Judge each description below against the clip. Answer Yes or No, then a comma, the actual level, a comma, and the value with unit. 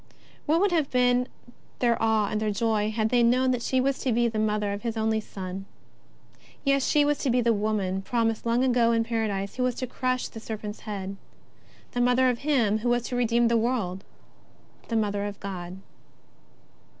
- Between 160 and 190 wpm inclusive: No, average, 200 wpm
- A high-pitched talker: Yes, high, 230 Hz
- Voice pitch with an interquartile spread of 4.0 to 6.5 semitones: No, average, 2.9 semitones